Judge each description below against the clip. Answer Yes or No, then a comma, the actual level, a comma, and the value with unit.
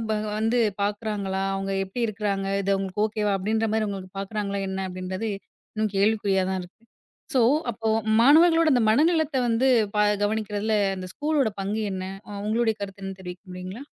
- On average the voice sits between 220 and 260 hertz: No, high, 210 Hz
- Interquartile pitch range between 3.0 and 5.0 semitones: No, narrow, 2.6 semitones